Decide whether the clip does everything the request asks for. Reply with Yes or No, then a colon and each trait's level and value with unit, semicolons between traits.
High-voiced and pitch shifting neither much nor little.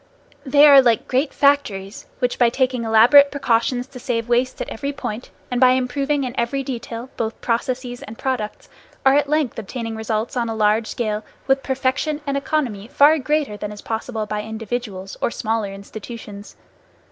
Yes: high, 245 Hz; average, 3.5 semitones